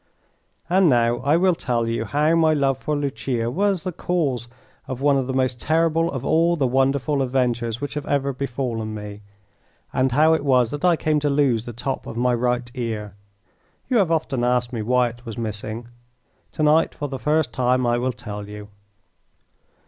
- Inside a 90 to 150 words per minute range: No, average, 195 wpm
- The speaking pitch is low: Yes, low, 130 Hz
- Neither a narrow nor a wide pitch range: Yes, average, 3.9 semitones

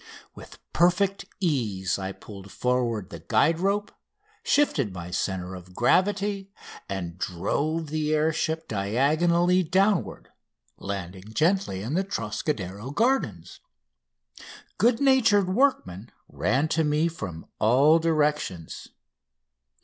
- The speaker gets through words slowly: Yes, slow, 110 wpm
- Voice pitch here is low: No, medium, 150 Hz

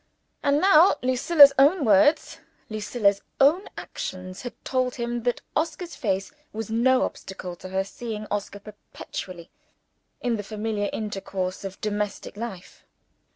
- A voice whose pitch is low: No, high, 220 Hz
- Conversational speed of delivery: No, slow, 130 wpm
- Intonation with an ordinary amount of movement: Yes, average, 4.7 semitones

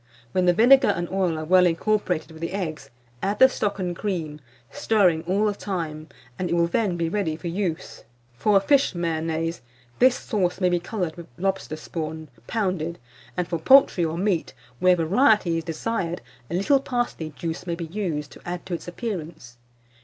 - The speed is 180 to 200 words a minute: Yes, average, 185 wpm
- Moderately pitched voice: Yes, medium, 175 Hz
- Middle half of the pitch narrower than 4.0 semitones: Yes, average, 3.6 semitones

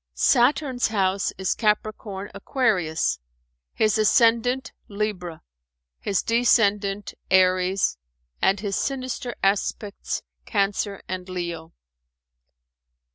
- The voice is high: Yes, high, 200 Hz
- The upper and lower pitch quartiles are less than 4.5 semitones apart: Yes, average, 3.3 semitones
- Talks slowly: Yes, slow, 80 wpm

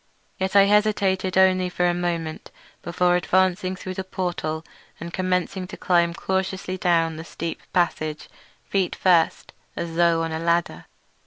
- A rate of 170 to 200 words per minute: No, average, 145 wpm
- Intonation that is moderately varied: No, narrow, 1.8 semitones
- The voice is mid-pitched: Yes, medium, 180 Hz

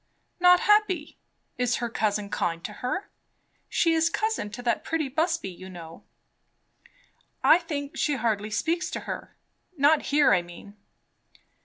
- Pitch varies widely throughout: Yes, wide, 7.9 semitones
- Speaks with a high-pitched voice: Yes, very high, 275 Hz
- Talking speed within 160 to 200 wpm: No, average, 145 wpm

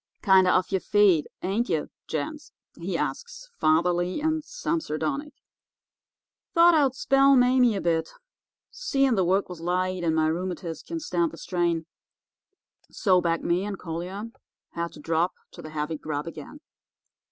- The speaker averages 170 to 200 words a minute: No, average, 150 wpm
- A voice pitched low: No, medium, 185 Hz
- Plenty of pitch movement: Yes, wide, 8.0 semitones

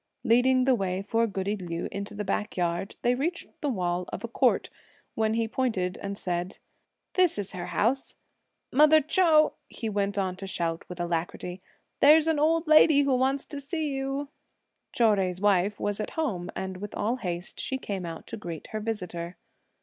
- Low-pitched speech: No, high, 210 Hz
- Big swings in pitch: Yes, wide, 6.7 semitones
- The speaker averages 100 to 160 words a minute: No, average, 180 wpm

